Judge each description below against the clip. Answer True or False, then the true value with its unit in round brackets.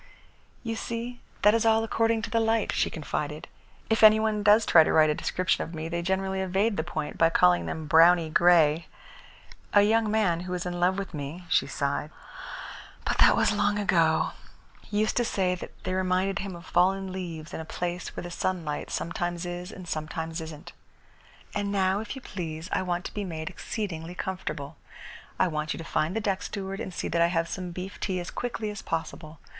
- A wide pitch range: False (3.8 semitones)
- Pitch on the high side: False (180 Hz)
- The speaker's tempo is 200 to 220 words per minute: True (205 wpm)